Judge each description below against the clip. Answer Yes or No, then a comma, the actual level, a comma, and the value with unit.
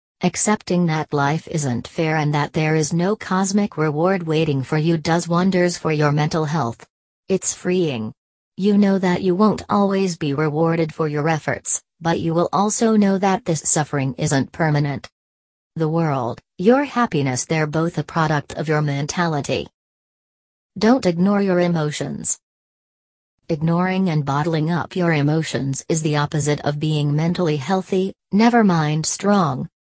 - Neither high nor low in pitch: Yes, medium, 160 Hz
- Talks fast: No, average, 150 wpm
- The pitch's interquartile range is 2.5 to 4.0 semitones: Yes, average, 3.4 semitones